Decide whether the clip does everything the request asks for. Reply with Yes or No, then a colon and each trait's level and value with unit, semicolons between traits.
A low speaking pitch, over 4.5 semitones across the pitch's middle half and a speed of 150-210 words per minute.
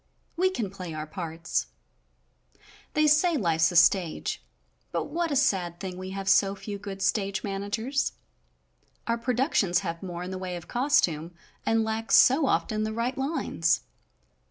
No: high, 195 Hz; wide, 5.6 semitones; average, 155 wpm